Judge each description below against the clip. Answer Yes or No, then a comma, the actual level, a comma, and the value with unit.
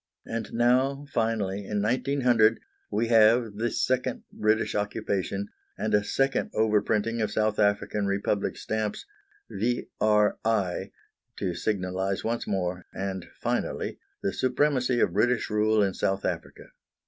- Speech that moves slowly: Yes, slow, 125 wpm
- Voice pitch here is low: Yes, low, 110 Hz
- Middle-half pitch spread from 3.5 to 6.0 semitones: No, narrow, 2.6 semitones